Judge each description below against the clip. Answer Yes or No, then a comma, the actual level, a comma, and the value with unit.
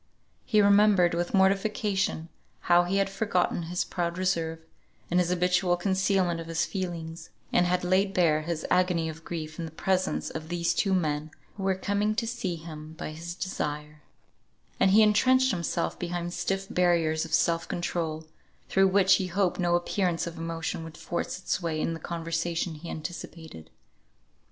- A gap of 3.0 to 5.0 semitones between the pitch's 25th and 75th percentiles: No, narrow, 2.6 semitones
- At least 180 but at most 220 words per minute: No, average, 170 wpm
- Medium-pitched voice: Yes, medium, 175 Hz